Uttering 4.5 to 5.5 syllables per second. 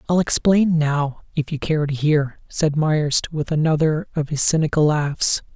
No: 4.2 syllables/s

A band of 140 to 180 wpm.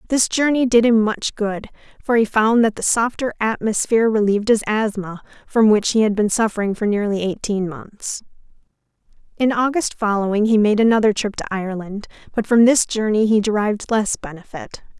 Yes: average, 170 wpm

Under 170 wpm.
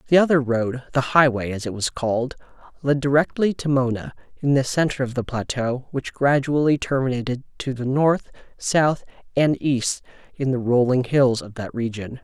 Yes: average, 160 wpm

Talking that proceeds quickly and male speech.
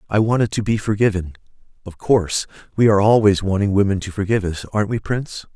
No: average, 185 wpm; male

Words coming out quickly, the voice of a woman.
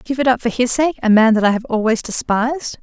Yes: fast, 255 wpm; female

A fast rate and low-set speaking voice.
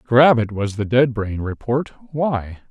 No: average, 180 wpm; low, 120 Hz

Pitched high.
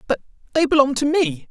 Yes: very high, 275 Hz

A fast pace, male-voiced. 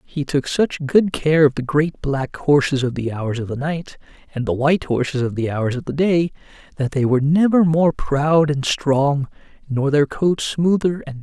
Yes: fast, 220 wpm; male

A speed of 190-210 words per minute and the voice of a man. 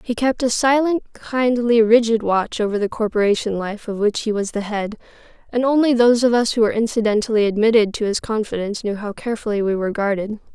No: average, 200 wpm; female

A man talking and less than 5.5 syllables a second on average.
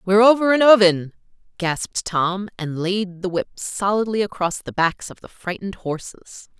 No: female; 4.8 syllables/s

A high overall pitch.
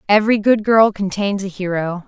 Yes: high, 200 Hz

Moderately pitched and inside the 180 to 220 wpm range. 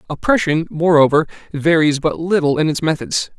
No: medium, 160 Hz; average, 140 wpm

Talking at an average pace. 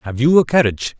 No: fast, 240 wpm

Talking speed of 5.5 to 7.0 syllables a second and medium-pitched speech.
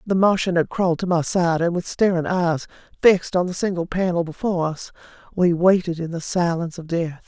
Yes: 5.6 syllables/s; medium, 175 Hz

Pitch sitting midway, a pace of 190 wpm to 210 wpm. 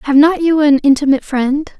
No: very high, 290 Hz; average, 200 wpm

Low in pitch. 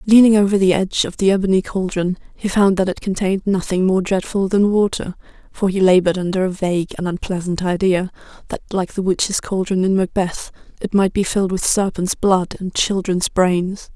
No: high, 190 Hz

